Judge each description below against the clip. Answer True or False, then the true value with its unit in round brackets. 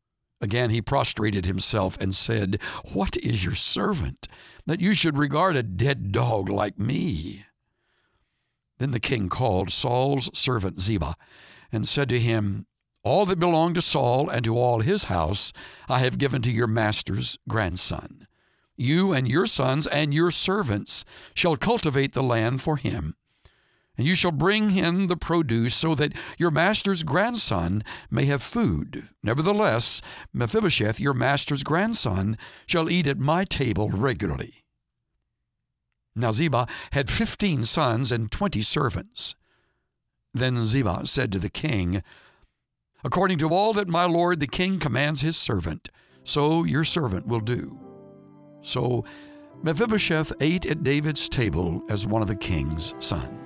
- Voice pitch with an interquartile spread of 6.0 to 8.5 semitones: True (7.0 semitones)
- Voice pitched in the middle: False (130 Hz)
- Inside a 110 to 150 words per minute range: True (145 wpm)